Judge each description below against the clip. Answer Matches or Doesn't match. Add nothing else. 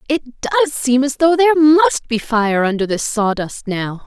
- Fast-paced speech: Doesn't match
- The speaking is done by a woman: Matches